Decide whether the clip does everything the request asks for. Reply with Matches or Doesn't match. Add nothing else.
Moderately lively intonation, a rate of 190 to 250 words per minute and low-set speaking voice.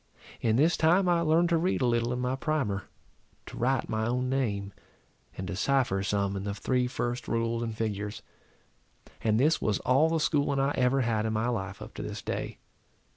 Matches